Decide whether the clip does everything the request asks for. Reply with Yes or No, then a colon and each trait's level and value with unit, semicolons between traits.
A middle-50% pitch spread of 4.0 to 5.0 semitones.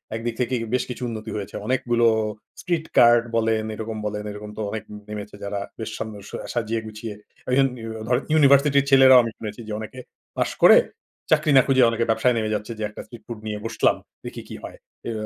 No: average, 2.8 semitones